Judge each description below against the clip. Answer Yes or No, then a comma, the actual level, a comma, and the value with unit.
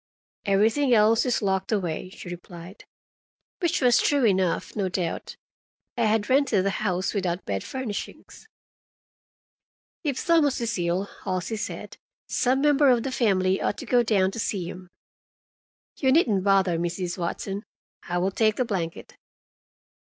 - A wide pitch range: No, average, 4.8 semitones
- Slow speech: No, average, 145 wpm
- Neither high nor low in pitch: No, high, 200 Hz